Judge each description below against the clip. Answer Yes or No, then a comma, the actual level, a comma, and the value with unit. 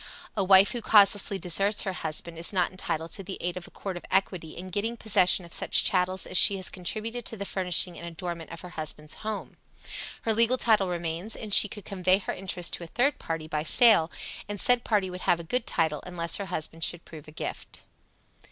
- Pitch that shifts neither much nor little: Yes, average, 3.3 semitones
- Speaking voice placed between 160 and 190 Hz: Yes, medium, 185 Hz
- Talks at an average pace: No, fast, 220 wpm